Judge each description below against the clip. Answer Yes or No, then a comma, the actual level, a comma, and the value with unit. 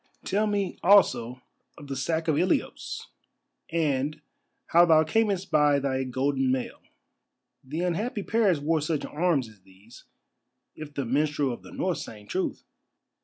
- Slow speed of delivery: No, average, 145 wpm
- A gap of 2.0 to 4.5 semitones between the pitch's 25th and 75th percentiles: No, average, 5.0 semitones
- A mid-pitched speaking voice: Yes, medium, 150 Hz